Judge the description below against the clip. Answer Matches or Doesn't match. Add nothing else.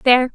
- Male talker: Doesn't match